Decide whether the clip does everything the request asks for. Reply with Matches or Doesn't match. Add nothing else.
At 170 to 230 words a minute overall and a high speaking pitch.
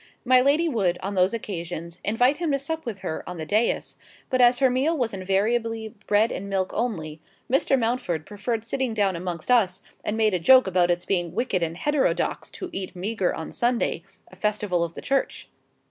Matches